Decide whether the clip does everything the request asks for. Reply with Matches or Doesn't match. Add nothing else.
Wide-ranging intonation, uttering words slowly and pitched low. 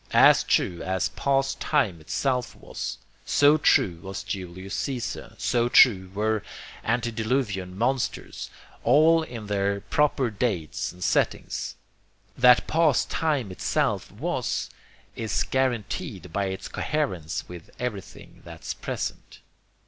Matches